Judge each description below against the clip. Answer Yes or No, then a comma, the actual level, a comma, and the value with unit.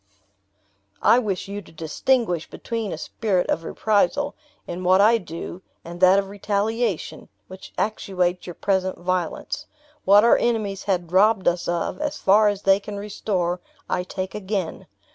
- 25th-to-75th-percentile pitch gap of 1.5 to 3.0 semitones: Yes, average, 2.7 semitones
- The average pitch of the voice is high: Yes, high, 195 Hz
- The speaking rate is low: No, average, 155 wpm